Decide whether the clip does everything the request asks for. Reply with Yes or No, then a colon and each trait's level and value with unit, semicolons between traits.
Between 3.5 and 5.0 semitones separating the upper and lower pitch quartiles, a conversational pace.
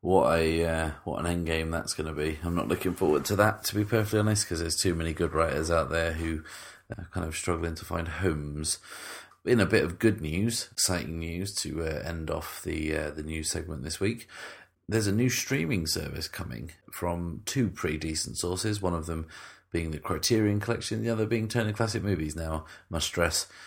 No: average, 4.6 semitones; fast, 210 wpm